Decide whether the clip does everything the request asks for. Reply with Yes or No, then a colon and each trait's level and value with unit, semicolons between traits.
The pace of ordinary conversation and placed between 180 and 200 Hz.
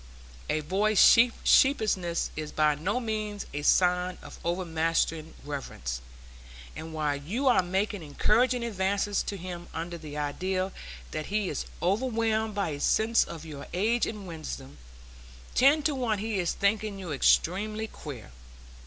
Yes: average, 145 wpm; medium, 185 Hz